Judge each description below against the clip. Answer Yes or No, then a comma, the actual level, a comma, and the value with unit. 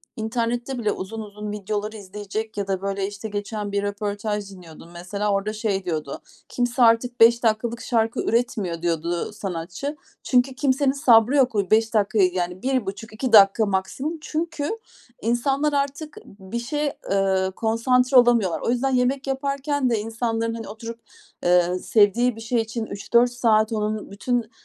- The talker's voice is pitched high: Yes, high, 220 Hz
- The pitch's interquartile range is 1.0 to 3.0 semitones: No, average, 3.5 semitones